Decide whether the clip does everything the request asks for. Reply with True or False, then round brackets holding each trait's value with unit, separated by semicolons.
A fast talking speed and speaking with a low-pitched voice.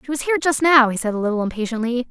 False (285 wpm; 255 Hz)